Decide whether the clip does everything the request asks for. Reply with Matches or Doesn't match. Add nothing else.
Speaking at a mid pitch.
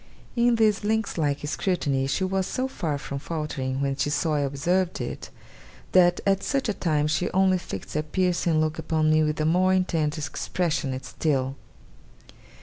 Matches